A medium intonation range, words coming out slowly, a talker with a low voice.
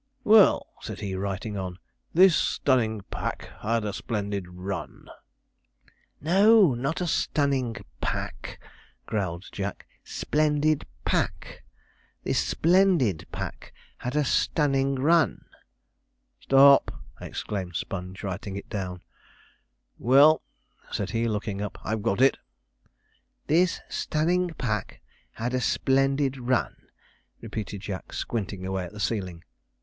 No: wide, 6.5 semitones; slow, 110 wpm; low, 115 Hz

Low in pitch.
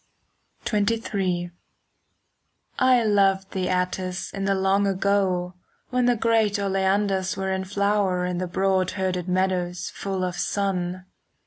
No: high, 190 Hz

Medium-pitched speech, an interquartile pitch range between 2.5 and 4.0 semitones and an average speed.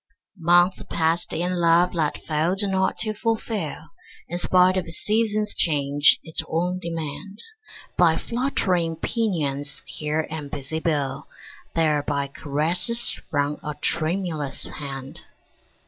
No: medium, 165 Hz; average, 3.6 semitones; slow, 115 wpm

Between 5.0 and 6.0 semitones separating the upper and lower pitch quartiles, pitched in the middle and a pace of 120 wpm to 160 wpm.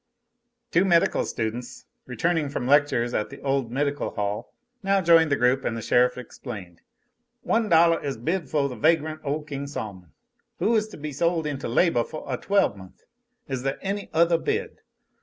No: average, 5.3 semitones; medium, 145 Hz; average, 175 wpm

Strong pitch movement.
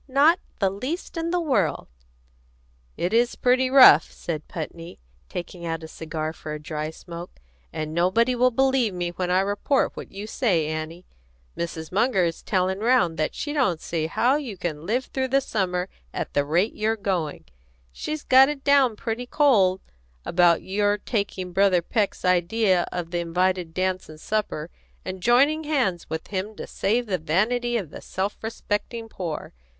Yes: wide, 6.1 semitones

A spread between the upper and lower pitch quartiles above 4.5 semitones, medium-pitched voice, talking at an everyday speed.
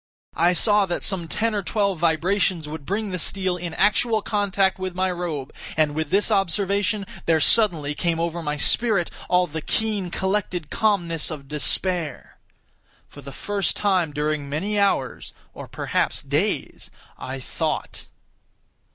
No: average, 4.2 semitones; medium, 180 Hz; average, 145 wpm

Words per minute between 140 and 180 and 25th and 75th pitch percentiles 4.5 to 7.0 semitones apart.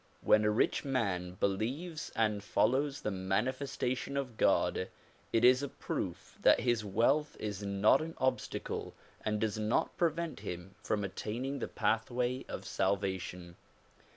Yes: average, 145 wpm; average, 4.8 semitones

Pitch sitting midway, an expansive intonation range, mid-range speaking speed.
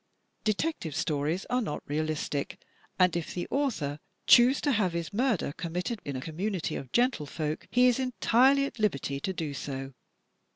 Yes: medium, 180 Hz; wide, 8.4 semitones; average, 165 wpm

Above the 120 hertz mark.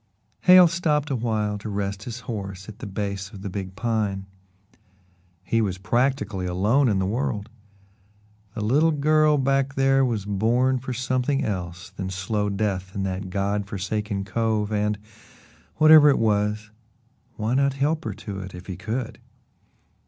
No: low, 105 Hz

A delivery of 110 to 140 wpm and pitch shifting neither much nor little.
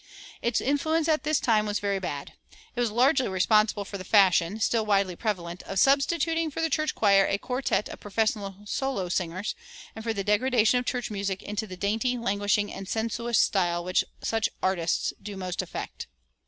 No: average, 180 wpm; average, 4.1 semitones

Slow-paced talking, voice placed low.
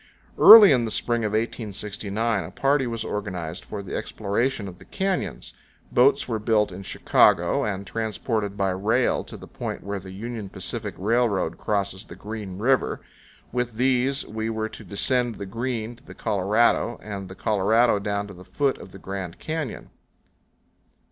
No: average, 170 wpm; low, 110 Hz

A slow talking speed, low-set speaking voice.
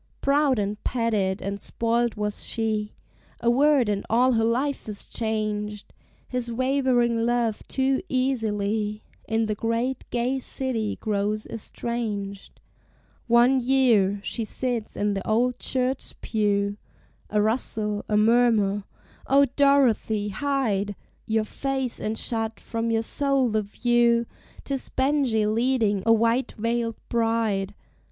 No: slow, 125 wpm; high, 230 Hz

